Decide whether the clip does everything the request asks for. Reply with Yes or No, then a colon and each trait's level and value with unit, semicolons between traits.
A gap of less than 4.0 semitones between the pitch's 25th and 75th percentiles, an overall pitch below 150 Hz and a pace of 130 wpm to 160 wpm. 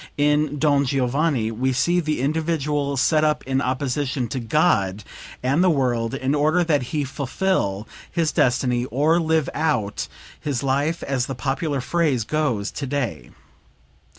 Yes: average, 3.4 semitones; medium, 140 Hz; average, 145 wpm